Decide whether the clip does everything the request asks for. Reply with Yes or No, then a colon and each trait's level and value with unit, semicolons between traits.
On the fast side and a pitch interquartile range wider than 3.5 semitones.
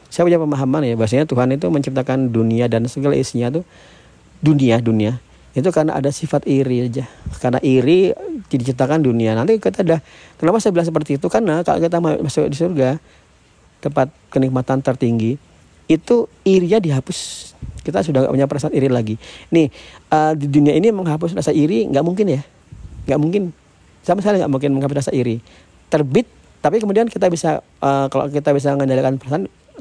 Yes: fast, 165 wpm; average, 4.0 semitones